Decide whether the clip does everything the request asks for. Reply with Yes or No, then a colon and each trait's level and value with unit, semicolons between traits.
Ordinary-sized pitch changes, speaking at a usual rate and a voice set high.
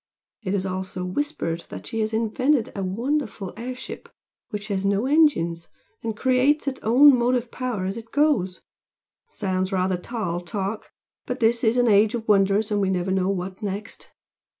Yes: average, 4.7 semitones; average, 175 wpm; high, 215 Hz